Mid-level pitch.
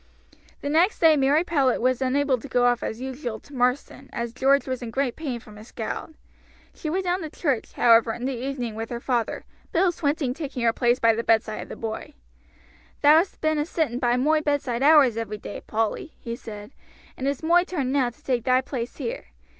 No: very high, 260 Hz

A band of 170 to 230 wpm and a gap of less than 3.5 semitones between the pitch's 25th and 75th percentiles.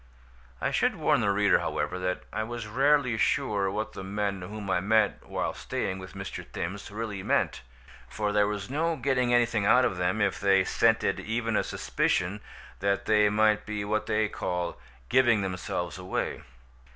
Yes: average, 175 wpm; narrow, 2.5 semitones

